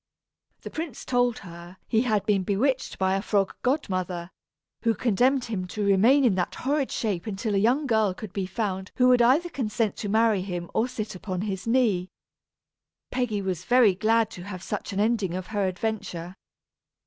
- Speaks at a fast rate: No, average, 185 wpm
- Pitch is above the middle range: Yes, high, 210 Hz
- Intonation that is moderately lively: Yes, average, 4.3 semitones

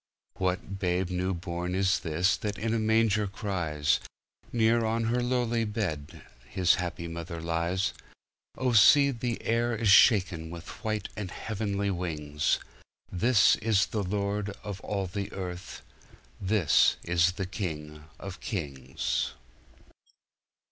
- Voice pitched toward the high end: No, very low, 95 Hz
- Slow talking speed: Yes, slow, 125 wpm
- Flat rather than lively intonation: No, average, 4.0 semitones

